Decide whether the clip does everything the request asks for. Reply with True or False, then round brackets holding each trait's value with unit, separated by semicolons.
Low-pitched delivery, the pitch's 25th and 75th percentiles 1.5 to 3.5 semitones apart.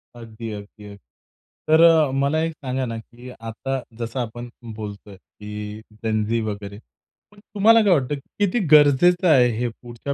False (120 Hz; 5.5 semitones)